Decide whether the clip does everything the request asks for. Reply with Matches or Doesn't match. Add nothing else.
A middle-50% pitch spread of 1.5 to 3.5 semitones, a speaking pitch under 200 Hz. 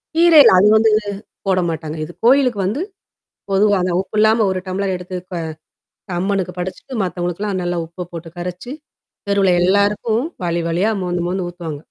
Matches